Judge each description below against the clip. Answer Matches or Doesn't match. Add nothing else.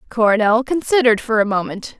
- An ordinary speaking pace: Matches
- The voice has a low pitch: Doesn't match